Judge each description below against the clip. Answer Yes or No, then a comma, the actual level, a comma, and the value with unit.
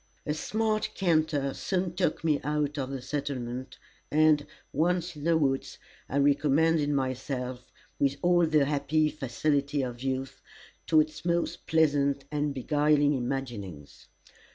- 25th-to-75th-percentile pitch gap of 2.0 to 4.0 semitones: Yes, narrow, 2.6 semitones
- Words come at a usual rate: No, slow, 130 wpm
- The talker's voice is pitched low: No, medium, 145 Hz